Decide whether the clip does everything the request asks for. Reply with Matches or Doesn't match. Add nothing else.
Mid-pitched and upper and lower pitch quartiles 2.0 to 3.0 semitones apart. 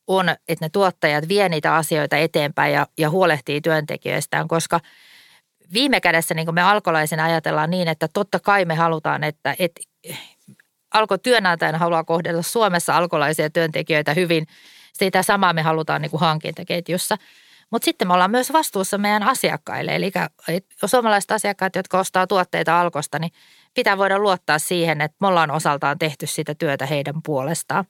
Doesn't match